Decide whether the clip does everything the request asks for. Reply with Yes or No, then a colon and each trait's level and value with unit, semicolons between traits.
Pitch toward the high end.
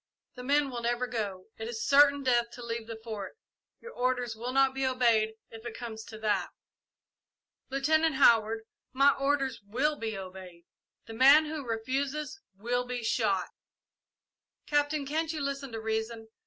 Yes: high, 245 Hz